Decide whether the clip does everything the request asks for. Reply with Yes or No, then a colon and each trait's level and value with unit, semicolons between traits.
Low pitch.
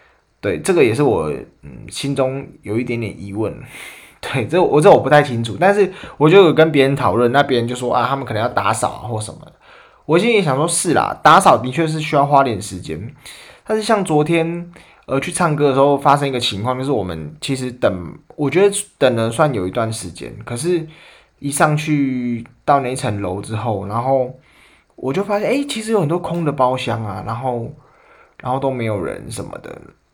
Yes: low, 130 Hz